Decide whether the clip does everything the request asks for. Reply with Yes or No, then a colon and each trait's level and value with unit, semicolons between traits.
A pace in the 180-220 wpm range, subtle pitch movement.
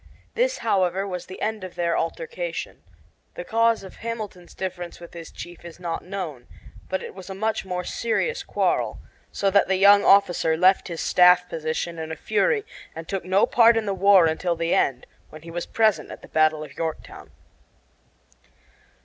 No: average, 185 wpm; average, 3.4 semitones